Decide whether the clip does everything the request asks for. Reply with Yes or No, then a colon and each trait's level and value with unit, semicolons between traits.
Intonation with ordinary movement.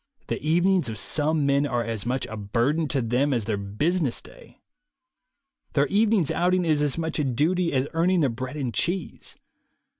No: wide, 5.7 semitones